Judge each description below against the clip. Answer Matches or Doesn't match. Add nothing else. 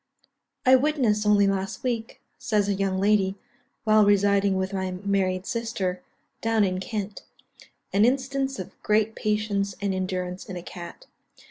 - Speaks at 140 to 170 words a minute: Matches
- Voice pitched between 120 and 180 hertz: Doesn't match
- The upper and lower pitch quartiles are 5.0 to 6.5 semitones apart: Doesn't match